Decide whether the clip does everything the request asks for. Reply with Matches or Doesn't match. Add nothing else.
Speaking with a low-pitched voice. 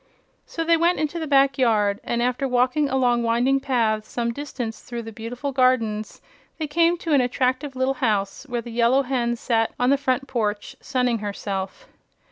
Doesn't match